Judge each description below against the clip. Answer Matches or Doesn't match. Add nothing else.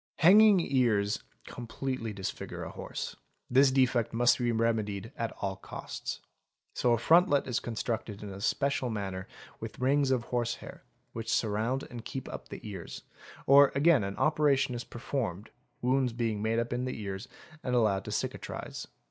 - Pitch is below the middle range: Matches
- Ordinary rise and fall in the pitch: Matches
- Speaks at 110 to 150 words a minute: Doesn't match